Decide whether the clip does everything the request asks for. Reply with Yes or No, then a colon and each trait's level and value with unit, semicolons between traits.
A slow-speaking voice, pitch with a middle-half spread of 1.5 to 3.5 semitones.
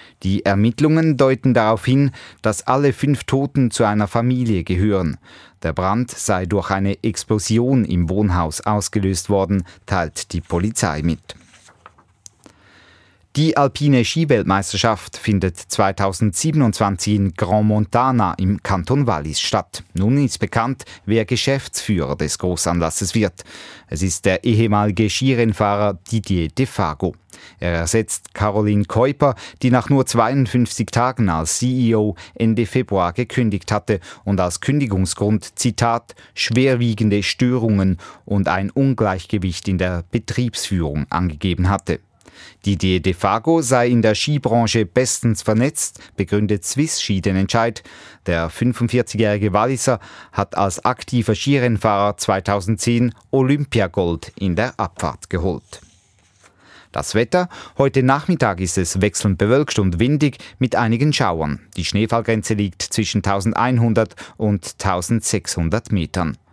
No: slow, 120 wpm; average, 4.1 semitones